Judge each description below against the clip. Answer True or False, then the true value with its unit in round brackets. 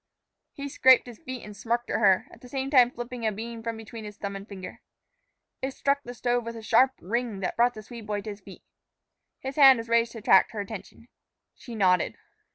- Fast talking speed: True (225 wpm)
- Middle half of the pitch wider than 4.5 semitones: False (2.8 semitones)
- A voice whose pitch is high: True (230 Hz)